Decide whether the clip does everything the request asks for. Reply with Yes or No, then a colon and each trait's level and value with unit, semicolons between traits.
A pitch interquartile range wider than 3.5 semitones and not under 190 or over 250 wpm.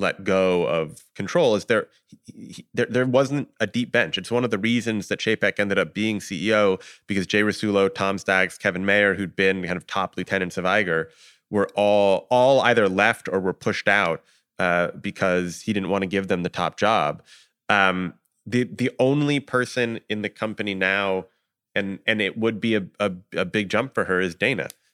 No: average, 2.8 semitones; average, 200 wpm